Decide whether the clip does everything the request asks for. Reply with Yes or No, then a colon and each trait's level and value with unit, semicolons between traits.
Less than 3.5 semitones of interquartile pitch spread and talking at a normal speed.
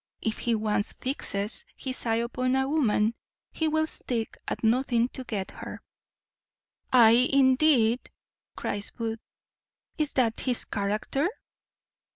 No: average, 3.1 semitones; slow, 125 wpm